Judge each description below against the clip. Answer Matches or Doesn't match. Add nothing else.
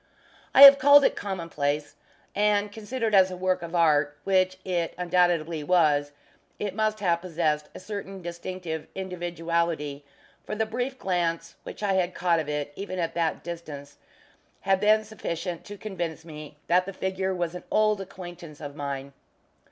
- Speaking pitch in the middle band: Matches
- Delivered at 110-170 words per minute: Matches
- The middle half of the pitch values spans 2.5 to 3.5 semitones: Matches